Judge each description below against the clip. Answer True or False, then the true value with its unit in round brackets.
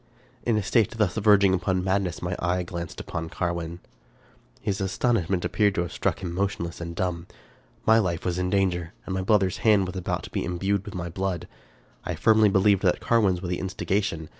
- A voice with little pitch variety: True (2.3 semitones)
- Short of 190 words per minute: False (195 wpm)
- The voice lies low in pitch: True (95 Hz)